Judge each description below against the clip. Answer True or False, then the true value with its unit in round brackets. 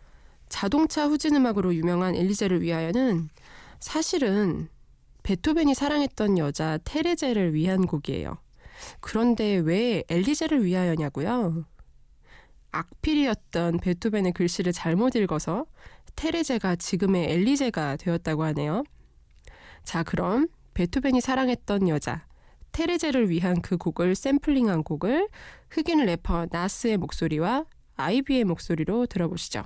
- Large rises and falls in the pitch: True (7.5 semitones)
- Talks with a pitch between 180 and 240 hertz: True (190 Hz)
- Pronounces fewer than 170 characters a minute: False (290 characters per minute)